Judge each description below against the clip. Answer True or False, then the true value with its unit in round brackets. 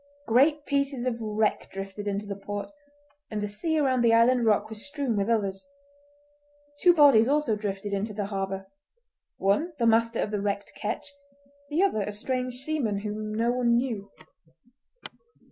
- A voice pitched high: True (220 Hz)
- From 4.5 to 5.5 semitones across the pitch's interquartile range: False (4.1 semitones)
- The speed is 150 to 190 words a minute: True (160 wpm)